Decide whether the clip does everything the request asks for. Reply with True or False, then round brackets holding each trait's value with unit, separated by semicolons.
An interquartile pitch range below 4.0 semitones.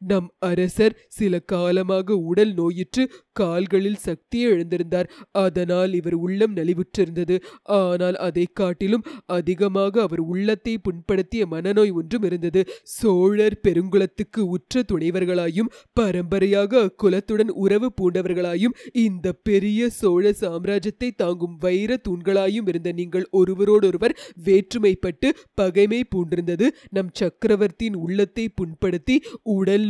True (2.9 semitones)